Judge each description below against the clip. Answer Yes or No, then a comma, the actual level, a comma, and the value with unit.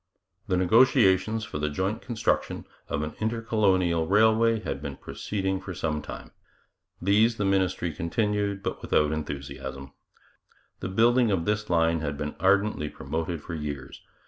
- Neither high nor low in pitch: No, very low, 95 Hz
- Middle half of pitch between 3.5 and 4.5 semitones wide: No, average, 5.0 semitones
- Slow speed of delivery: No, average, 145 wpm